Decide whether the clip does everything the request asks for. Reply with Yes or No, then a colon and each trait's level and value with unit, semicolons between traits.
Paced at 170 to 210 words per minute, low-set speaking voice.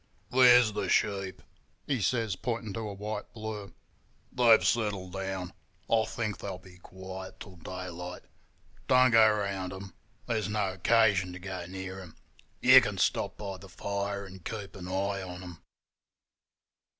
No: average, 150 wpm; low, 100 Hz